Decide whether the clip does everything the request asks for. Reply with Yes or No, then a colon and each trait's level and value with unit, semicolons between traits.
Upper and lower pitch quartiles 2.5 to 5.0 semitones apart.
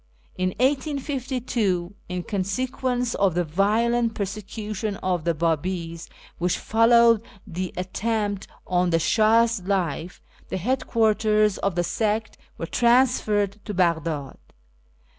Yes: average, 4.3 semitones